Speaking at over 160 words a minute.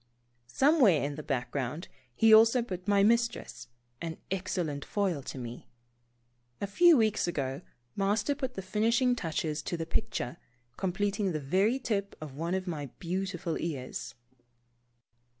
No: average, 140 wpm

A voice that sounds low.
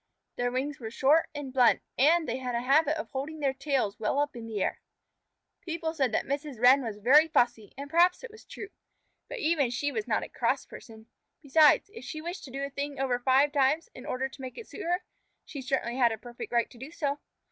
No: very high, 275 Hz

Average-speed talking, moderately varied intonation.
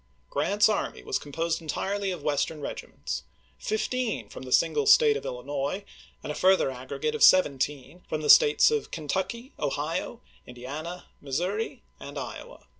No: average, 150 wpm; wide, 7.0 semitones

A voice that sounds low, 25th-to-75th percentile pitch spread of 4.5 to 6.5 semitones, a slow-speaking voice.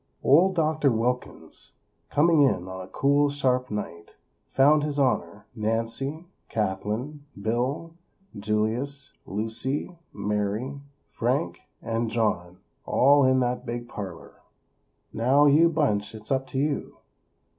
Yes: low, 125 Hz; average, 5.0 semitones; slow, 115 wpm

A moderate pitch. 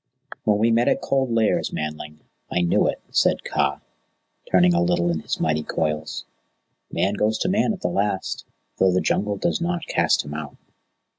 No: very low, 95 Hz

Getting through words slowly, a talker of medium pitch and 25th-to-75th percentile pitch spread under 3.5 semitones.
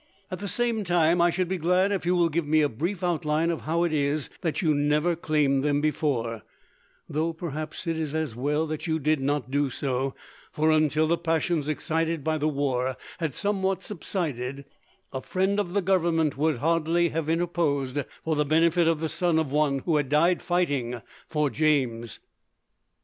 No: average, 190 wpm; medium, 155 Hz; average, 2.9 semitones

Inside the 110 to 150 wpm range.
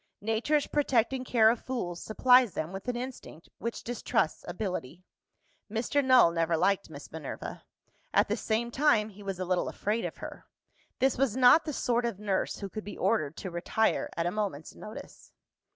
No: average, 180 wpm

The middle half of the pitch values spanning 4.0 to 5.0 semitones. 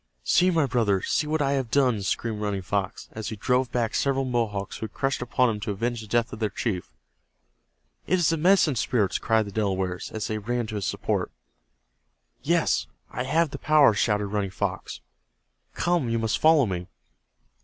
Yes: average, 4.7 semitones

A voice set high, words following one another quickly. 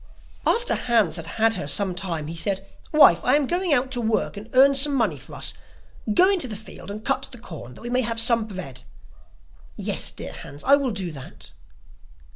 Yes: high, 225 Hz; fast, 210 wpm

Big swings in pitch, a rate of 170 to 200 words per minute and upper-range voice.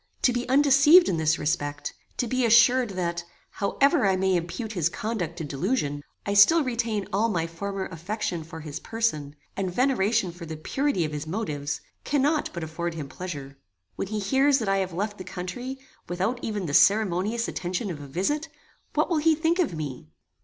Yes: wide, 6.6 semitones; average, 190 wpm; high, 195 Hz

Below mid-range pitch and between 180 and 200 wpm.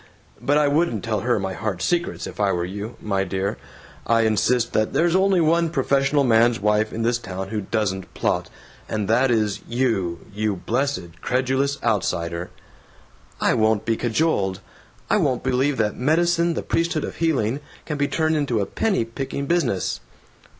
No: low, 115 Hz; average, 170 wpm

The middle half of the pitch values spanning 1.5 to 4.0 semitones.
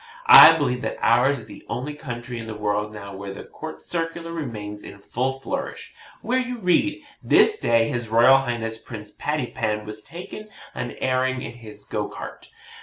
No: wide, 5.6 semitones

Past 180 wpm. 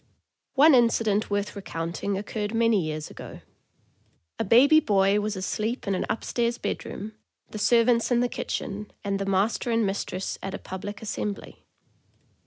No: average, 160 wpm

